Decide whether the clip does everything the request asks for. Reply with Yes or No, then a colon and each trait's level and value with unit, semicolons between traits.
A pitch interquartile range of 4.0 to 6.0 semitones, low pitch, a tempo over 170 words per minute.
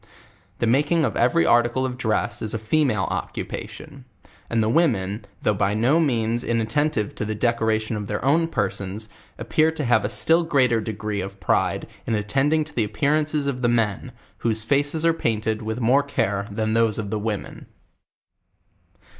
Yes: average, 4.7 semitones; low, 115 Hz; average, 180 wpm